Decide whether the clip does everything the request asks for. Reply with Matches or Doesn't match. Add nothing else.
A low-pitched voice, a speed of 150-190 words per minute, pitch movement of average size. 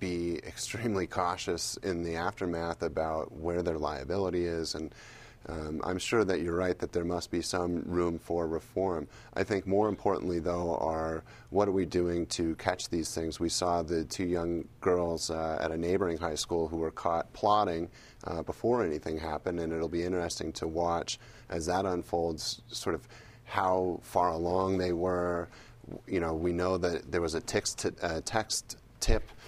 Doesn't match